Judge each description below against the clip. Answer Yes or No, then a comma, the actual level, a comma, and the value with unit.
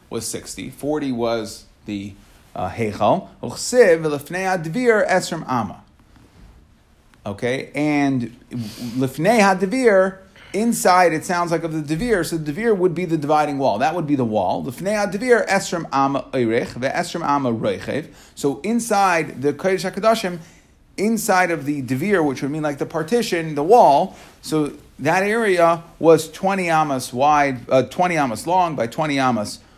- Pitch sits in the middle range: Yes, medium, 155 Hz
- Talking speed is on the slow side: Yes, slow, 120 wpm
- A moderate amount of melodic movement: No, wide, 5.9 semitones